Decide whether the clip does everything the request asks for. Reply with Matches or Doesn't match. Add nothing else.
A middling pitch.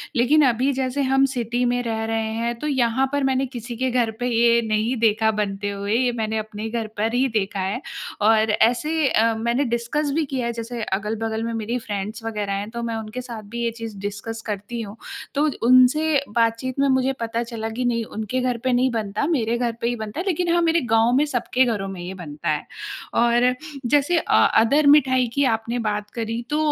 Doesn't match